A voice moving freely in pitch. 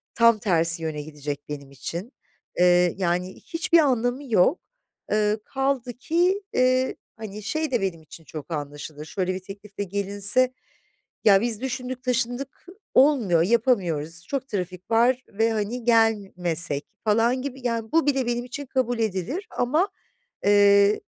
Yes: wide, 5.9 semitones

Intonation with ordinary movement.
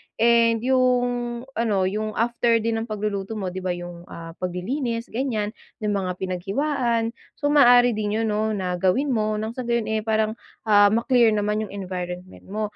Yes: average, 3.4 semitones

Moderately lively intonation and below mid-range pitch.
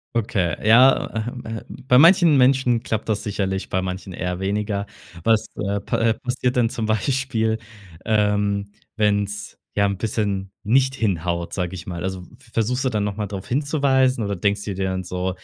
Yes: average, 4.0 semitones; low, 105 Hz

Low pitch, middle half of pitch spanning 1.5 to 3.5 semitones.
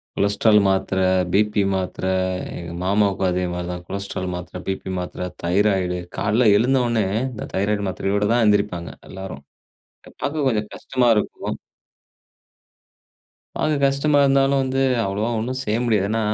No: low, 105 Hz; average, 3.9 semitones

